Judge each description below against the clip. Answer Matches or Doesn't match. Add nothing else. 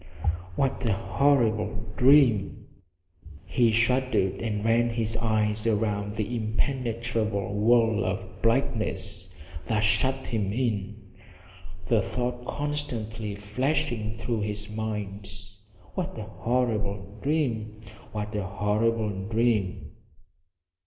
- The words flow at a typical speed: Doesn't match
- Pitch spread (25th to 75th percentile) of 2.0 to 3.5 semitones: Matches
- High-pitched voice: Doesn't match